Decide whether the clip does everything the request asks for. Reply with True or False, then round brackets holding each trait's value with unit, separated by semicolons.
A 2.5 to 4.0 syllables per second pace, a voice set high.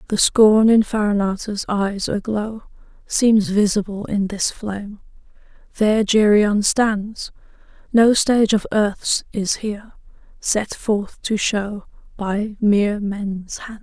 True (3.7 syllables/s; 210 Hz)